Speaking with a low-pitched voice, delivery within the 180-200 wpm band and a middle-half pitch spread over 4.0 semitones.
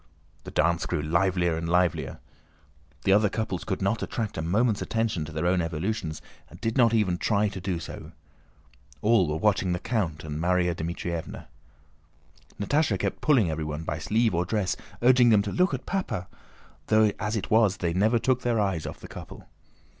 Yes: very low, 95 Hz; average, 185 wpm; average, 4.5 semitones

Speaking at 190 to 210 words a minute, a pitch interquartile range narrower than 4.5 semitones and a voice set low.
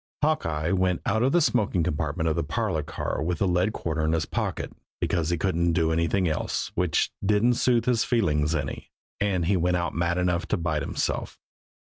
Yes: average, 195 wpm; average, 3.5 semitones; very low, 85 Hz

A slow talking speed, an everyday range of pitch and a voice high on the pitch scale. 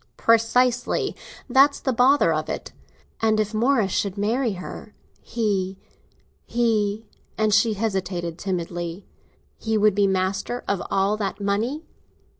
Yes: slow, 115 wpm; average, 3.2 semitones; high, 215 Hz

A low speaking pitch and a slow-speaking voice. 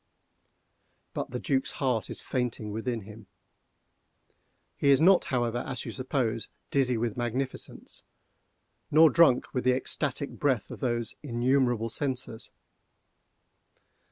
Yes: low, 125 Hz; slow, 120 wpm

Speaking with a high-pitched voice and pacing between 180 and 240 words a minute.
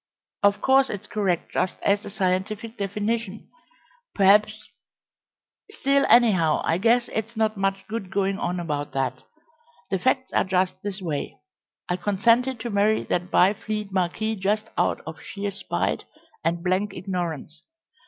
No: high, 200 Hz; average, 145 wpm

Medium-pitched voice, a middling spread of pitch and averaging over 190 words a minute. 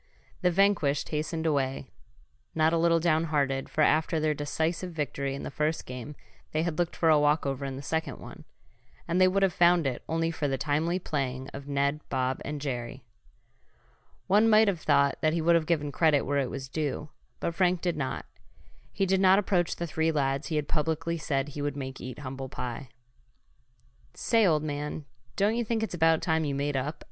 Yes: medium, 155 Hz; average, 3.3 semitones; average, 200 wpm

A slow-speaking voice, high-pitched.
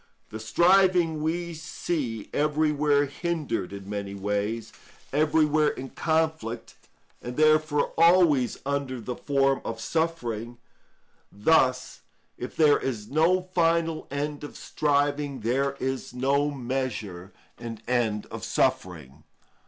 No: slow, 115 wpm; medium, 140 Hz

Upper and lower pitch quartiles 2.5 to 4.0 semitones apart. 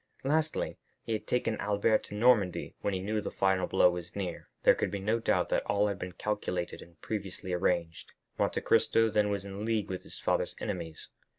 Yes: average, 2.9 semitones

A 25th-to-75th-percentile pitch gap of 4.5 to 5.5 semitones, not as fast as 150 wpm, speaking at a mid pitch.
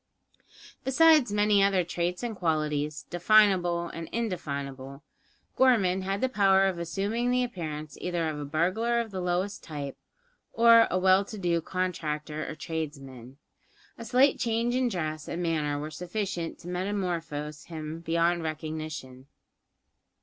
Yes: average, 4.8 semitones; average, 140 wpm; medium, 175 Hz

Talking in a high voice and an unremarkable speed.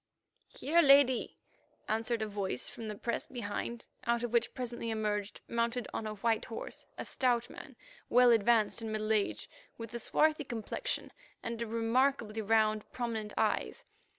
Yes: high, 230 Hz; average, 150 wpm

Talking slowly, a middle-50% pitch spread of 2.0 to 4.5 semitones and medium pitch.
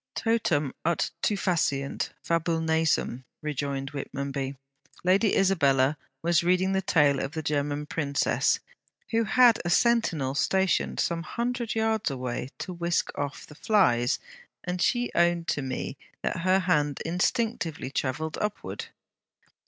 No: slow, 130 wpm; average, 5.2 semitones; medium, 165 Hz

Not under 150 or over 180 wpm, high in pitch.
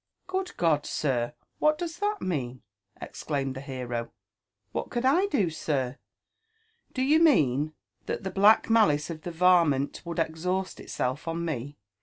No: average, 160 wpm; medium, 165 Hz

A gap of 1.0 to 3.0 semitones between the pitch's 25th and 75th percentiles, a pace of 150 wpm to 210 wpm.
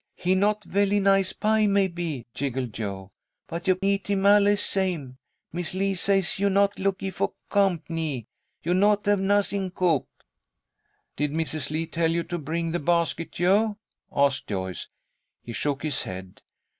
No: average, 4.8 semitones; average, 155 wpm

